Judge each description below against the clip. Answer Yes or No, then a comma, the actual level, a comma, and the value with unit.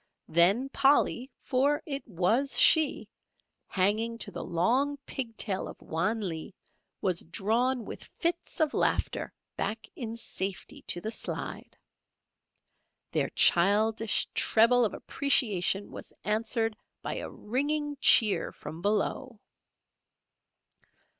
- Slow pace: Yes, slow, 115 wpm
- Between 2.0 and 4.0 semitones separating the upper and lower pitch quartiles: No, average, 5.0 semitones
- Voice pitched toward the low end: No, high, 225 Hz